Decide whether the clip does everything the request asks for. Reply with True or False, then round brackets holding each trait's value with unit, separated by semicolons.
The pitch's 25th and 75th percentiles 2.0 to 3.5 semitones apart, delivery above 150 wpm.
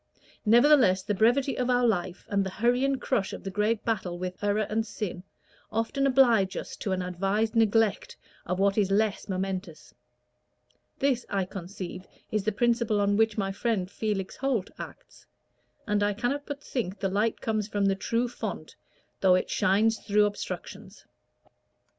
True (3.1 semitones; 165 wpm)